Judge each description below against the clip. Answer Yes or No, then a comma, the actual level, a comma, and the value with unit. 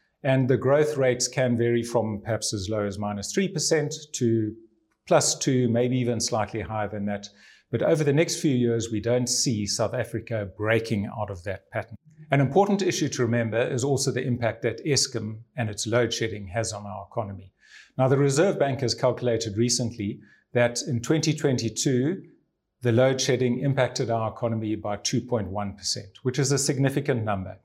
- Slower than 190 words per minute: Yes, average, 175 wpm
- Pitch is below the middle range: Yes, low, 120 Hz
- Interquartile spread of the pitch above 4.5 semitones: No, average, 3.6 semitones